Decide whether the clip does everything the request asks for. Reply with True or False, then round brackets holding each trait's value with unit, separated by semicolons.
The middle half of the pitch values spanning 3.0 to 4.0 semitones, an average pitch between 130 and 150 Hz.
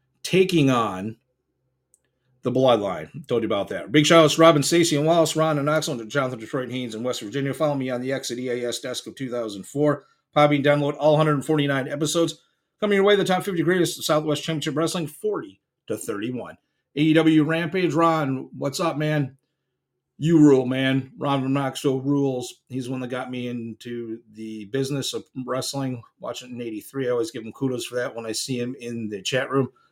True (3.7 semitones; 135 Hz)